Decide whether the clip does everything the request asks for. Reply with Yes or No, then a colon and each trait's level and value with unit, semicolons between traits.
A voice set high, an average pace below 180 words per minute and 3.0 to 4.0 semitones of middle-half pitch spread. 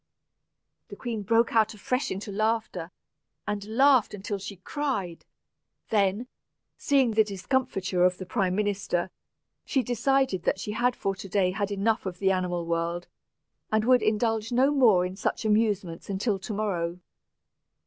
Yes: high, 205 Hz; average, 150 wpm; average, 3.5 semitones